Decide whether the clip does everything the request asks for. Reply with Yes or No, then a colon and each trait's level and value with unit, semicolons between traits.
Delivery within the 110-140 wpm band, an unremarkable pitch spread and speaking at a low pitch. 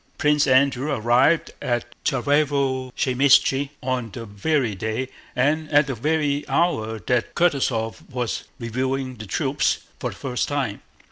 Yes: slow, 135 wpm; average, 3.1 semitones; low, 130 Hz